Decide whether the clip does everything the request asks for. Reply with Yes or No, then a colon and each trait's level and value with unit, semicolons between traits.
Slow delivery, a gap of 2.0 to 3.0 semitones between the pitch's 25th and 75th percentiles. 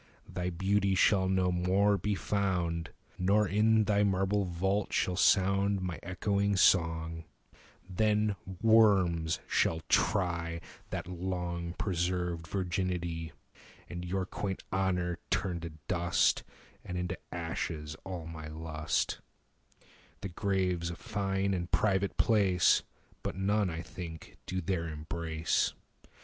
Yes: slow, 125 wpm; narrow, 2.5 semitones